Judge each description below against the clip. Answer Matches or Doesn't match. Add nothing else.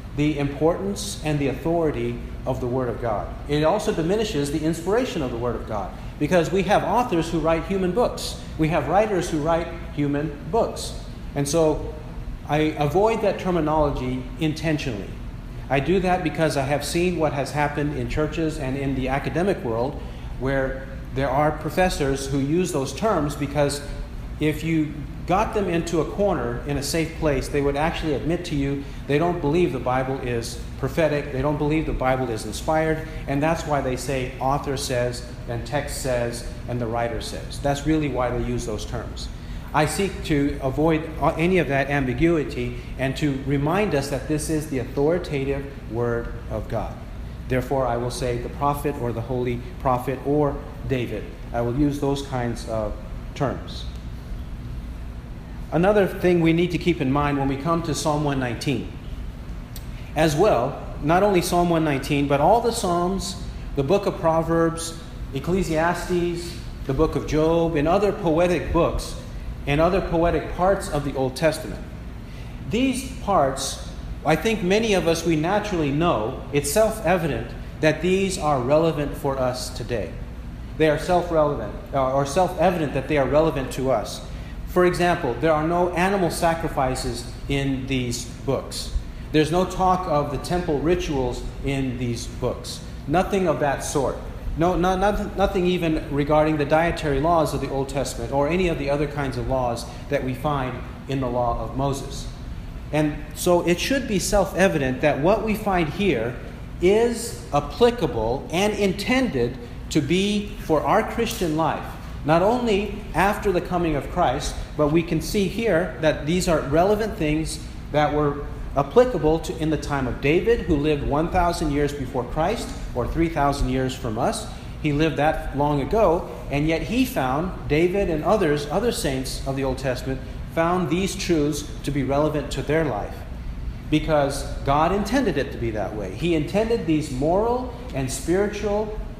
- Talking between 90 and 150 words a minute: Doesn't match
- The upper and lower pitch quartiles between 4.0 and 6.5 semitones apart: Matches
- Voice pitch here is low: Doesn't match